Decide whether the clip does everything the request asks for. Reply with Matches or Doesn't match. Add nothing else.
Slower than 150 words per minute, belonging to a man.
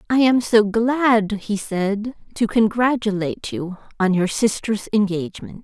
Doesn't match